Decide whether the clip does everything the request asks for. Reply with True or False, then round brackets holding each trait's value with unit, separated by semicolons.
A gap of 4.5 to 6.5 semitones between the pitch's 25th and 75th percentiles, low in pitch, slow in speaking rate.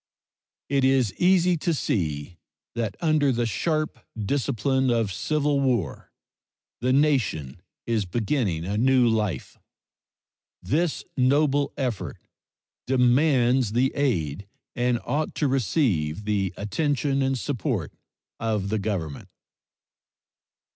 True (5.6 semitones; 125 Hz; 105 wpm)